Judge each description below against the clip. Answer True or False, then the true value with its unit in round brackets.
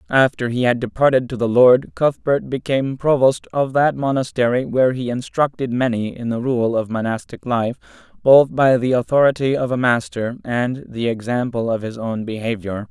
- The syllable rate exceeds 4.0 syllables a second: True (5.0 syllables/s)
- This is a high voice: False (125 Hz)